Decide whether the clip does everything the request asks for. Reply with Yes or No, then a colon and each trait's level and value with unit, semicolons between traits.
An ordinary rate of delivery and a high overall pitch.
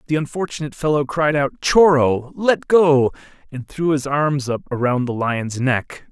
No: average, 165 wpm; medium, 140 Hz